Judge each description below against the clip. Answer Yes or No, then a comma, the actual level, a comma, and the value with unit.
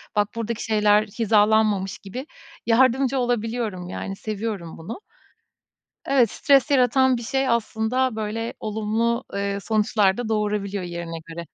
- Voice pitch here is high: Yes, high, 220 Hz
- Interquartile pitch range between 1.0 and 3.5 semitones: Yes, average, 2.9 semitones